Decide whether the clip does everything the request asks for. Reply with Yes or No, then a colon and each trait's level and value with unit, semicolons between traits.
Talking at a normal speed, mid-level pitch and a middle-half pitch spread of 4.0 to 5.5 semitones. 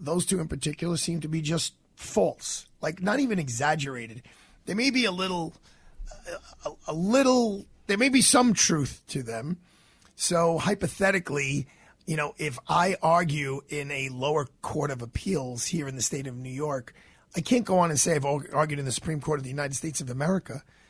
Yes: average, 190 wpm; medium, 155 Hz; average, 4.3 semitones